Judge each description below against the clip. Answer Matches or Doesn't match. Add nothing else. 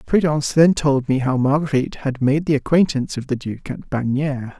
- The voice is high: Doesn't match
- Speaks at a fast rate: Doesn't match